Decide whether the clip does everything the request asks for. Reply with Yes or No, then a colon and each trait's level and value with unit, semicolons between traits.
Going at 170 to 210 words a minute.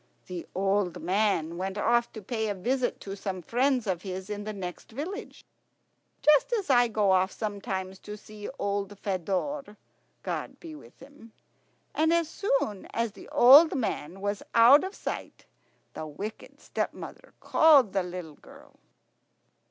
No: average, 150 wpm